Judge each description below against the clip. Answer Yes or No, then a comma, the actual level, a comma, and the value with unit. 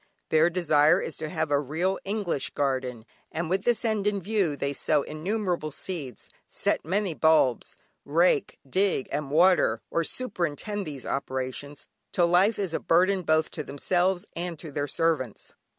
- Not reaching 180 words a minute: Yes, average, 160 wpm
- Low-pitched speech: No, medium, 165 Hz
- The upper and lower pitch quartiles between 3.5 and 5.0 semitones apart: Yes, average, 4.5 semitones